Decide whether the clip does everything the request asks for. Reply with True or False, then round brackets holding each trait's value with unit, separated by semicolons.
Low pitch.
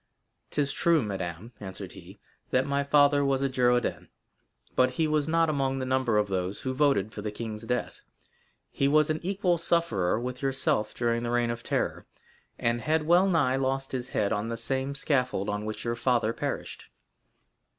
True (130 Hz)